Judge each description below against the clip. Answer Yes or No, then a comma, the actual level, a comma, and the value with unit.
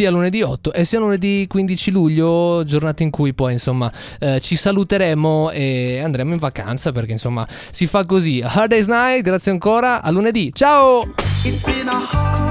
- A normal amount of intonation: No, wide, 7.1 semitones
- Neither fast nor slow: Yes, average, 160 wpm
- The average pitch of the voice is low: No, medium, 165 Hz